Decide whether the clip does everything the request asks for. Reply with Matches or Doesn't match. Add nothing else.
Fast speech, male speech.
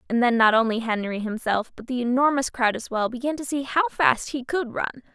Doesn't match